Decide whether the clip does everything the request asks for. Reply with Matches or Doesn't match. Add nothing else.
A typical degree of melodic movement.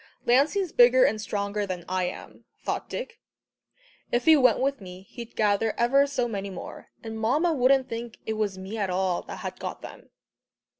Matches